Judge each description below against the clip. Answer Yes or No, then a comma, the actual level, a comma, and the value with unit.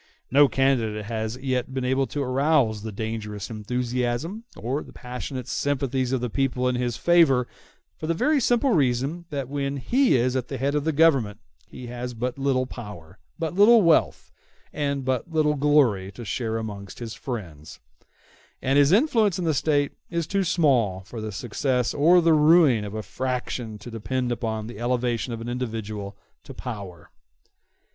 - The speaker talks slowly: No, average, 175 wpm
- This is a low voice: Yes, low, 125 Hz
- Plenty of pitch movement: No, average, 4.4 semitones